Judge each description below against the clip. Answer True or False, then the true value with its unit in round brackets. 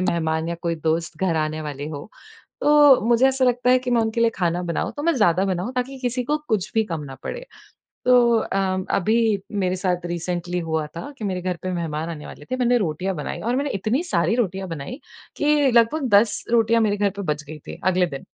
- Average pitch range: False (6.2 semitones)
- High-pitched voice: True (195 Hz)